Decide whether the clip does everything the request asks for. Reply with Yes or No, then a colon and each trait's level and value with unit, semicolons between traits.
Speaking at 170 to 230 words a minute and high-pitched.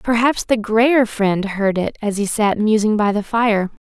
Yes: average, 200 wpm; high, 215 Hz